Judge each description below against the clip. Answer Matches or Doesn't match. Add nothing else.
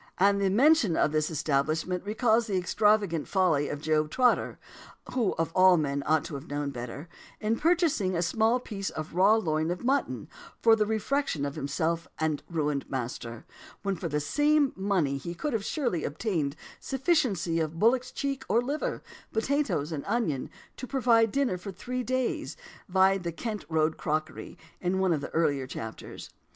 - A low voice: Doesn't match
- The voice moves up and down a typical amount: Doesn't match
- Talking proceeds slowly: Doesn't match